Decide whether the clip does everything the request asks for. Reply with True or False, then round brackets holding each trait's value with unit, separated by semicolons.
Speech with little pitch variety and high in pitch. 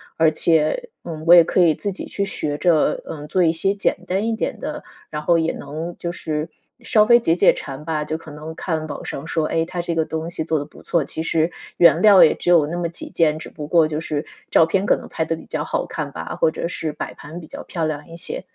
False (2.1 semitones; 165 Hz)